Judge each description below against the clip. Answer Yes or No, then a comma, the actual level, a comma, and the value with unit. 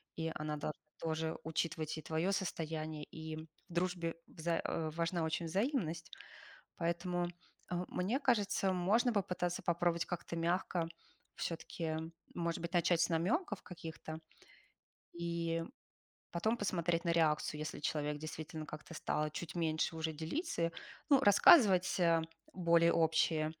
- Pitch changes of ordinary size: No, narrow, 2.0 semitones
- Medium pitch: Yes, medium, 170 Hz